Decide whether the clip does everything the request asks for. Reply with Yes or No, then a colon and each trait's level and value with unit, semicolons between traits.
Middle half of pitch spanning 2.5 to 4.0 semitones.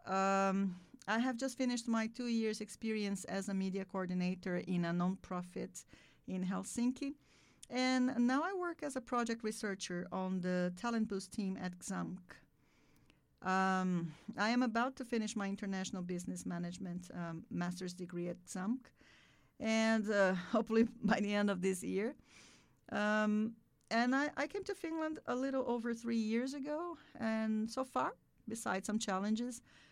No: average, 4.4 semitones